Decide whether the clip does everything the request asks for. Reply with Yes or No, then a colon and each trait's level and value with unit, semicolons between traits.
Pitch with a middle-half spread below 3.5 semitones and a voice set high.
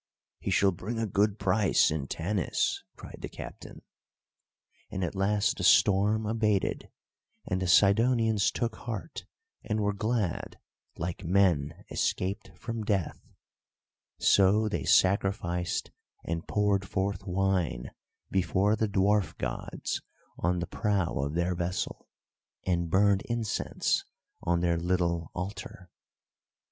No: average, 2.9 semitones; very low, 95 Hz